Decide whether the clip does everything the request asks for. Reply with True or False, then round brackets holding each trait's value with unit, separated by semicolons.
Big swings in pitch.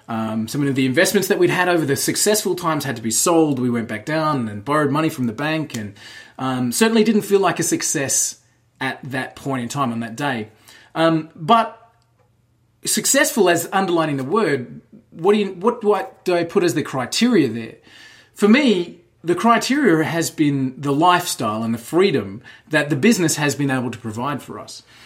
True (7.2 semitones)